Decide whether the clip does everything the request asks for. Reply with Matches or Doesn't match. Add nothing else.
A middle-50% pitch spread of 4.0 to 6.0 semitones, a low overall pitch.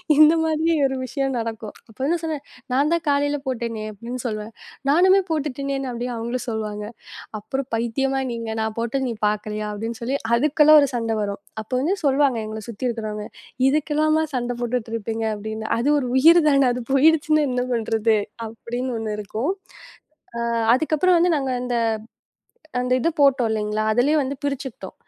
Doesn't match